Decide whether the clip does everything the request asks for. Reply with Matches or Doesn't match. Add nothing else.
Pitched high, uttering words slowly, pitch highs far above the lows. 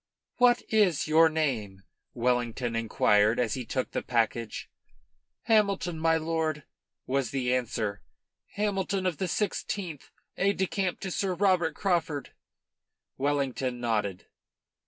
Doesn't match